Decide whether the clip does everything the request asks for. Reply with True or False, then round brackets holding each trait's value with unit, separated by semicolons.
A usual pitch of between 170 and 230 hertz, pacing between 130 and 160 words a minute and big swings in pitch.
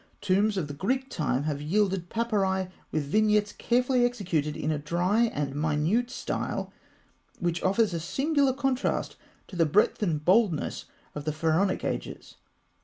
True (190 Hz; 150 wpm; 6.3 semitones)